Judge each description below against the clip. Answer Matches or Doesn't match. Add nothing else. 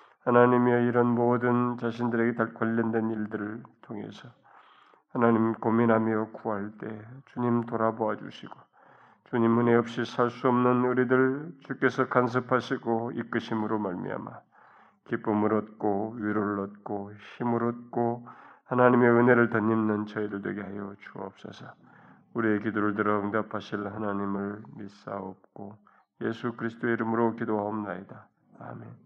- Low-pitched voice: Matches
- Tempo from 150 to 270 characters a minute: Doesn't match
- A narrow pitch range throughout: Matches